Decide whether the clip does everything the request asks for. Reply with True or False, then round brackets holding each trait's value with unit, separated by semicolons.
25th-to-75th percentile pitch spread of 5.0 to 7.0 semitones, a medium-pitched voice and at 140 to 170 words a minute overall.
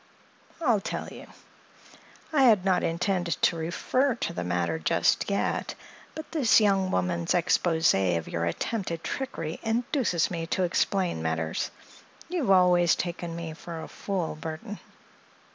False (4.6 semitones; 175 Hz; 145 wpm)